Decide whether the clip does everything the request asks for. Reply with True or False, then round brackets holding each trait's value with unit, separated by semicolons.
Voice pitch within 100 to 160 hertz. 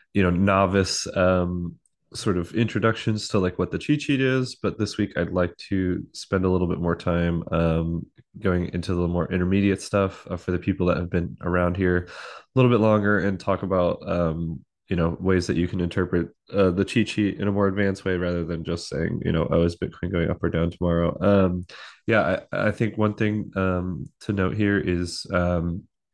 False (90 Hz)